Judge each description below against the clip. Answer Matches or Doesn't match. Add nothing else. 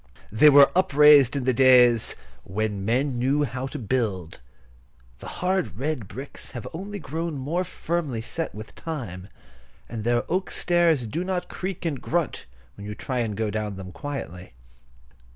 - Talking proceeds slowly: Doesn't match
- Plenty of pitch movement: Matches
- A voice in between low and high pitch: Doesn't match